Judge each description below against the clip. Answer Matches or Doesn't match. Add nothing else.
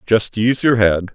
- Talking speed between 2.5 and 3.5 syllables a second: Doesn't match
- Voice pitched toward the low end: Matches